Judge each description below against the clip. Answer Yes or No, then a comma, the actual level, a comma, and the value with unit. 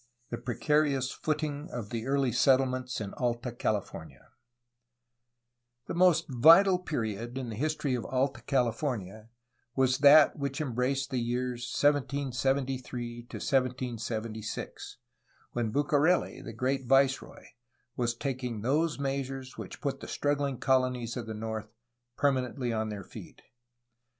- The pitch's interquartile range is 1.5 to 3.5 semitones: Yes, average, 3.0 semitones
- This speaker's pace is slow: Yes, slow, 125 wpm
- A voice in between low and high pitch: No, low, 130 Hz